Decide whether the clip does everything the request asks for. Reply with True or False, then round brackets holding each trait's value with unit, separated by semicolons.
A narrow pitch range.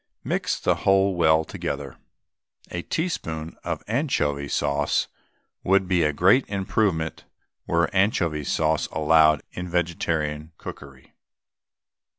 False (3.8 semitones)